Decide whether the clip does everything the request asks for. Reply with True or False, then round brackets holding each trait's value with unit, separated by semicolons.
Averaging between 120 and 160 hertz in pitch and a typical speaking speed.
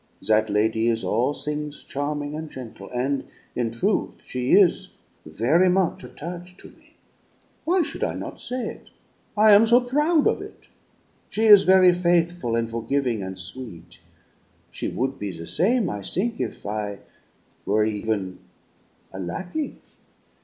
True (140 Hz; 150 wpm)